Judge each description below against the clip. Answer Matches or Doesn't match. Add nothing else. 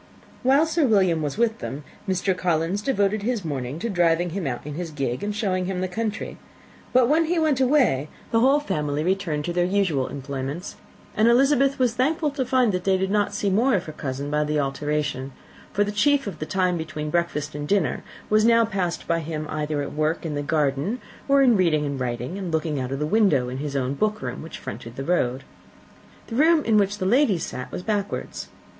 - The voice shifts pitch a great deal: Matches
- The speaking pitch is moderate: Matches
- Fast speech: Matches